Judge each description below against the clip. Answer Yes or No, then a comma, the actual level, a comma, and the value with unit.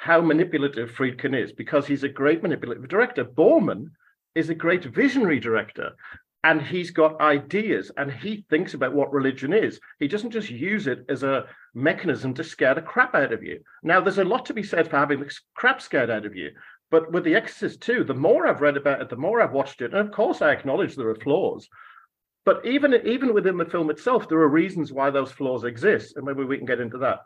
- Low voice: No, medium, 150 Hz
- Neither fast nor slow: No, fast, 225 wpm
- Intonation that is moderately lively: Yes, average, 4.0 semitones